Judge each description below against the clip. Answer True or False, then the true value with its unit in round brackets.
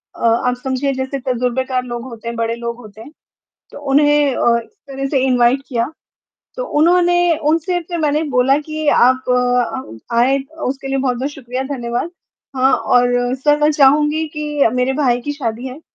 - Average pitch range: True (3.0 semitones)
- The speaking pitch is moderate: False (265 Hz)